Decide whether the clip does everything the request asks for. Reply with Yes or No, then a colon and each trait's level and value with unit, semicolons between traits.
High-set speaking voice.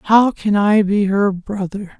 Yes: high, 200 Hz